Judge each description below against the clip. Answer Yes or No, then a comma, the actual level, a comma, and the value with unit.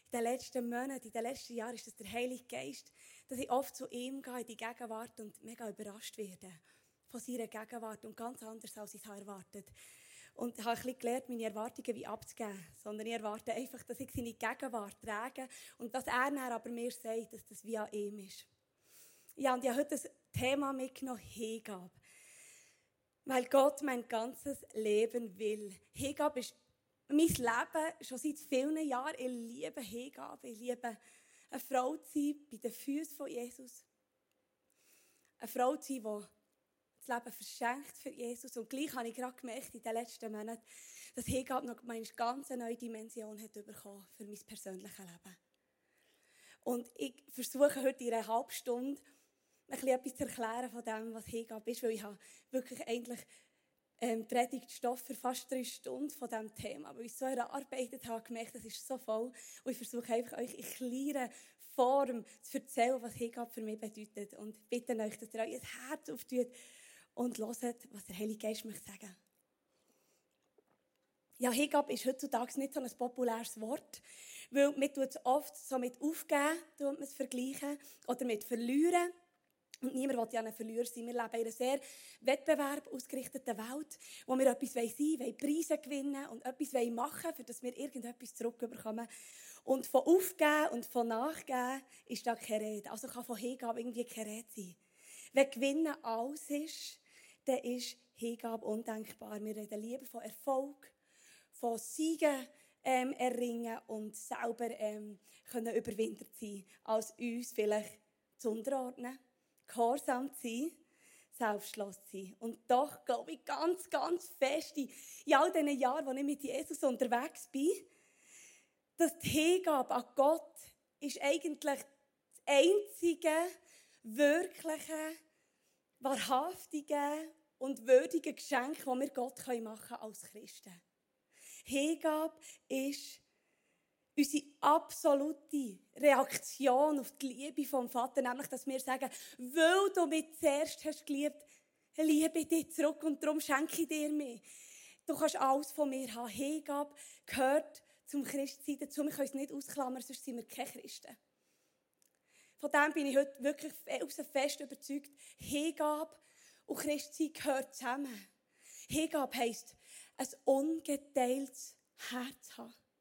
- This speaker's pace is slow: No, average, 155 wpm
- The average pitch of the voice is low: No, very high, 255 Hz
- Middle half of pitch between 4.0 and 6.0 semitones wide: No, average, 3.5 semitones